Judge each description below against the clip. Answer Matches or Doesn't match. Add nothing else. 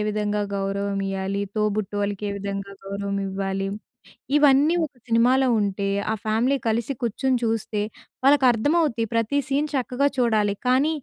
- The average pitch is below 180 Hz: Doesn't match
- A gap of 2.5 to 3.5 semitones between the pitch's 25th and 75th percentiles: Doesn't match